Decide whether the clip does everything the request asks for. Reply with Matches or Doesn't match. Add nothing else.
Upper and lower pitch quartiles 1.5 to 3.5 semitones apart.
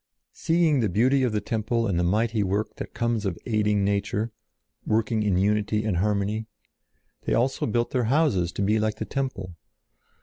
Matches